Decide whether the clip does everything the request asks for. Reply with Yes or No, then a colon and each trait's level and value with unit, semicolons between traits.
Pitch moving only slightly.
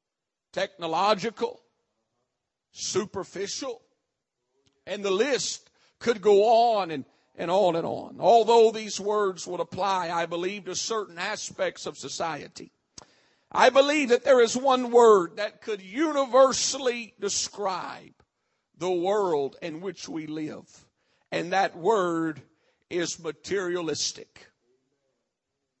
No: average, 5.3 semitones